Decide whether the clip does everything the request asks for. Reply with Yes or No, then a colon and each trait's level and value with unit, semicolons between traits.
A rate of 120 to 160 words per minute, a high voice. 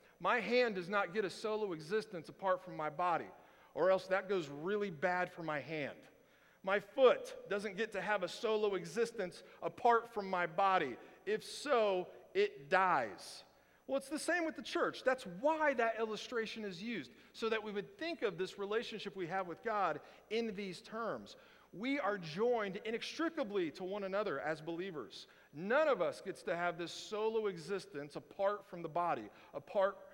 No: average, 175 wpm; high, 205 Hz